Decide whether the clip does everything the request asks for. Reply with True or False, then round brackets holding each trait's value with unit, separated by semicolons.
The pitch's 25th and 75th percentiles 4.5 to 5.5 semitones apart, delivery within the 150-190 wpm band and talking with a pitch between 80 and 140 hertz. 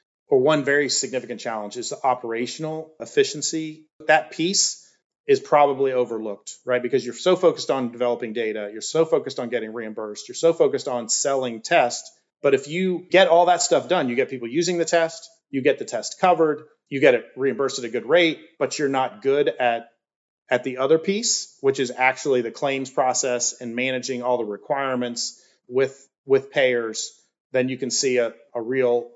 True (4.8 semitones; 185 wpm; 135 Hz)